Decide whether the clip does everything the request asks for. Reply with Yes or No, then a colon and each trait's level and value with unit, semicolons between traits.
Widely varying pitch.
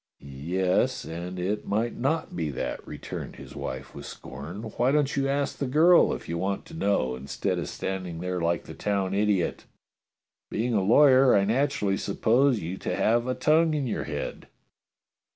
Yes: wide, 7.0 semitones